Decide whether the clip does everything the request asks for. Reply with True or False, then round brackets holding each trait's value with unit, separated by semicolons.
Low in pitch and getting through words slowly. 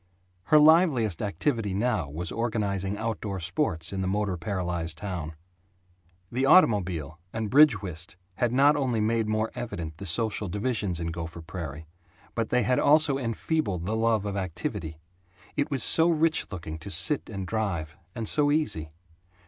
False (105 Hz; 155 wpm)